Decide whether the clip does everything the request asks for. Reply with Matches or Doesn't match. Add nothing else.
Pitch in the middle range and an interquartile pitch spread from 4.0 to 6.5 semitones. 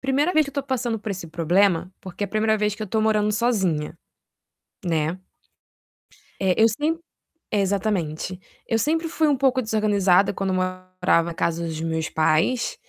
Doesn't match